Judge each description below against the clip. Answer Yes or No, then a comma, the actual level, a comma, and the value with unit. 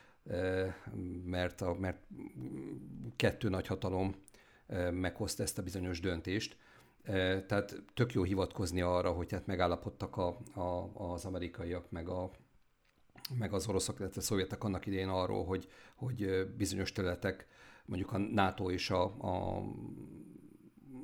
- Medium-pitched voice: No, very low, 95 Hz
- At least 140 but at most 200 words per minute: No, average, 125 wpm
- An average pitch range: No, narrow, 1.7 semitones